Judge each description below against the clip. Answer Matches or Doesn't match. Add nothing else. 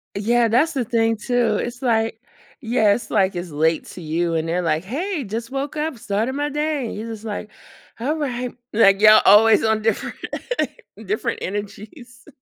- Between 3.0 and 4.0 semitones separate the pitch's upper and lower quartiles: Matches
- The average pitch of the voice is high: Matches